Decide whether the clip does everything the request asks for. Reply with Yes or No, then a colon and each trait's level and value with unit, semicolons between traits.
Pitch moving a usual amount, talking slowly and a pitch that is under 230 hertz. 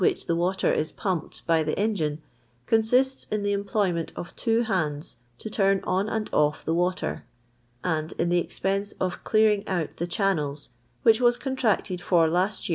No: average, 4.2 semitones; average, 175 wpm; high, 190 Hz